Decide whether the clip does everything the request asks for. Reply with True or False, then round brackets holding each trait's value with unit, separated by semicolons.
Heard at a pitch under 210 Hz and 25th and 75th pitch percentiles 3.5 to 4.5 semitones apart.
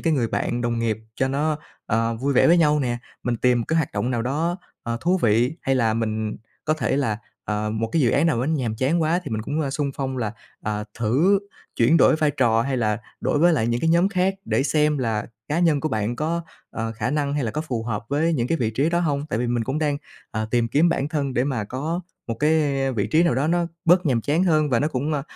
False (135 Hz; 5.1 semitones)